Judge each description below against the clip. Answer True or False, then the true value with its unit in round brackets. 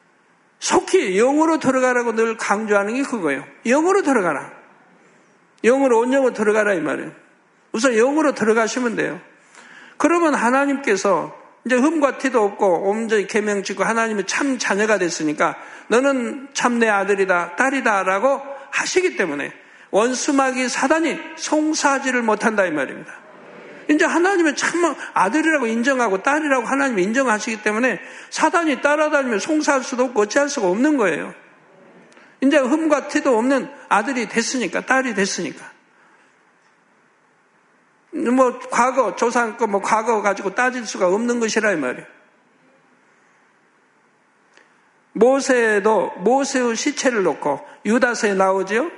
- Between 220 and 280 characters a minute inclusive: False (310 characters per minute)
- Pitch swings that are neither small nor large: True (4.5 semitones)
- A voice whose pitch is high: True (255 Hz)